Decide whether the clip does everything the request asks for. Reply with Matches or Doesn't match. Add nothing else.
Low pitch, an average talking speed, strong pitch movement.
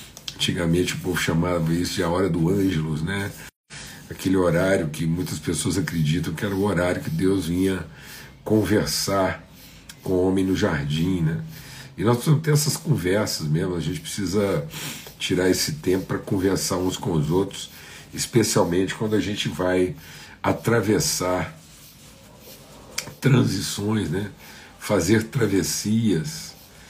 Doesn't match